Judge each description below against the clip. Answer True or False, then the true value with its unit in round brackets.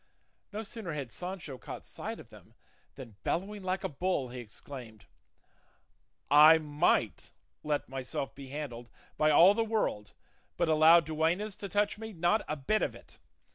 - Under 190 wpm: True (160 wpm)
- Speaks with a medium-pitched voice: True (155 Hz)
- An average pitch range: False (6.0 semitones)